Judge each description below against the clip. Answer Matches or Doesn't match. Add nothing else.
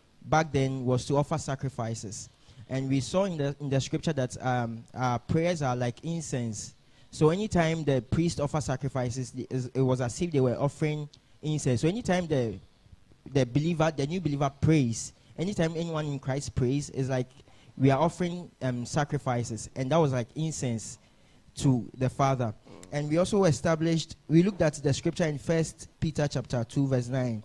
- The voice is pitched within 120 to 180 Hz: Matches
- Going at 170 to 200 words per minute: Matches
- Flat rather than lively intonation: Doesn't match